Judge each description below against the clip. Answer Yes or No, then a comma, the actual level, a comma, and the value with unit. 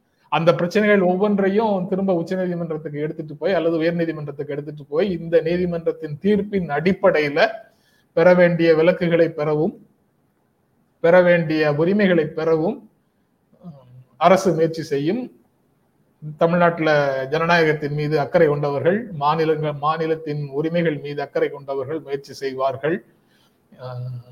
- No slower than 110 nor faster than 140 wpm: No, average, 100 wpm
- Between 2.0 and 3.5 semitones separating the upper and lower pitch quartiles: Yes, average, 3.1 semitones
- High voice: No, medium, 160 Hz